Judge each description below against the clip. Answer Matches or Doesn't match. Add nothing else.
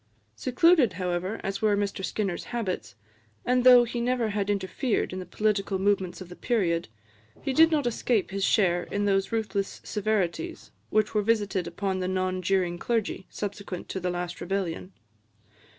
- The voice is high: Matches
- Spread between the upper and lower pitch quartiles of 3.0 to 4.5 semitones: Matches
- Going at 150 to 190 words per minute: Matches